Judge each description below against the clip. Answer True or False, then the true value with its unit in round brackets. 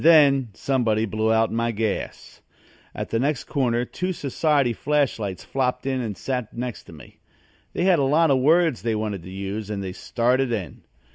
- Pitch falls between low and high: False (120 Hz)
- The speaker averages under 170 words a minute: False (195 wpm)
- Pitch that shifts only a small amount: False (4.2 semitones)